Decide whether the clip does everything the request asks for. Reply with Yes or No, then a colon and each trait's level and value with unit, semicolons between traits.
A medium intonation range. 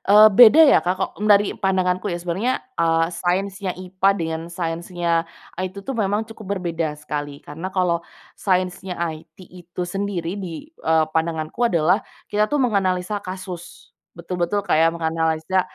Yes: average, 3.0 semitones